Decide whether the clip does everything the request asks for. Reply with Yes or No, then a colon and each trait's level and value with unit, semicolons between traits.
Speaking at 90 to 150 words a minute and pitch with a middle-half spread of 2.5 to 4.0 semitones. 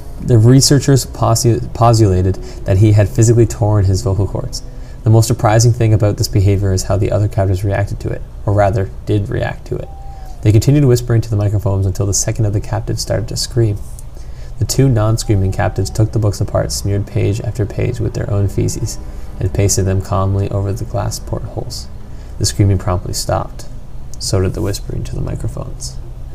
No: average, 190 wpm; average, 3.1 semitones